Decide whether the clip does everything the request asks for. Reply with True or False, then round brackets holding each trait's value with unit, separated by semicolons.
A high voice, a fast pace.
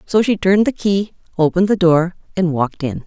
False (180 Hz; 215 wpm)